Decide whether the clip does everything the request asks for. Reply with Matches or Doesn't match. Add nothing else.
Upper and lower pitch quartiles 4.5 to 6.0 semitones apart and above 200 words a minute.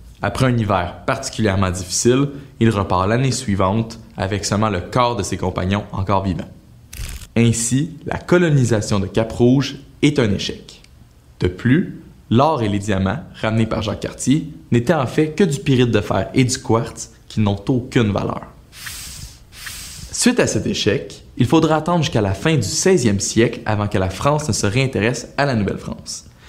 Doesn't match